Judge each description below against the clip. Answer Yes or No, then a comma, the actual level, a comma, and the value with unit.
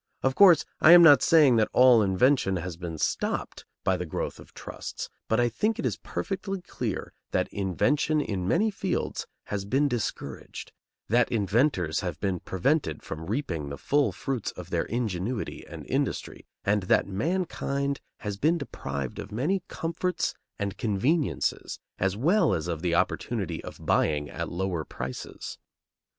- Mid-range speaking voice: No, low, 110 Hz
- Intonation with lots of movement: Yes, wide, 8.2 semitones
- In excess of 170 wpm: No, average, 160 wpm